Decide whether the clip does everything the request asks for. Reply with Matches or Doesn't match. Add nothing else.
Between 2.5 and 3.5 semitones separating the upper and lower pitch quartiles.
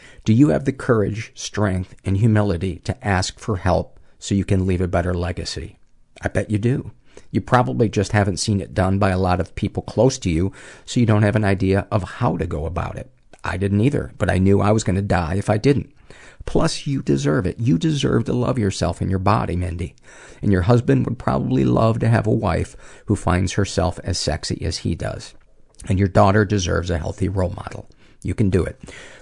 Matches